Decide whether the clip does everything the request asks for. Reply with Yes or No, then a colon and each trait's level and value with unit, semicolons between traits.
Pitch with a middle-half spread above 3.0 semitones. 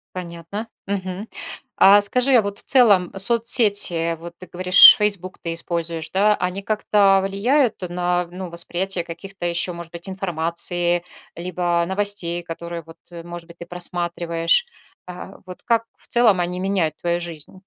No: average, 2.7 semitones